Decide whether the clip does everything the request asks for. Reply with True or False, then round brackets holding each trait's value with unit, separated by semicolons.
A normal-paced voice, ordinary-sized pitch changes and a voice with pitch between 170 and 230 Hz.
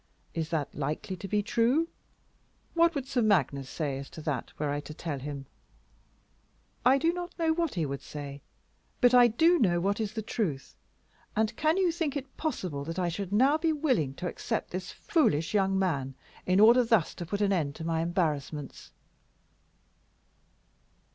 False (180 wpm; 8.8 semitones; 190 Hz)